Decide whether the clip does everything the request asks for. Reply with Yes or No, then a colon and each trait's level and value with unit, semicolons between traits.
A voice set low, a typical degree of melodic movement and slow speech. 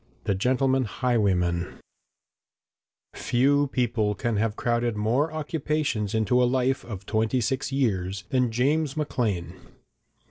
Yes: low, 120 Hz; average, 4.1 semitones; slow, 120 wpm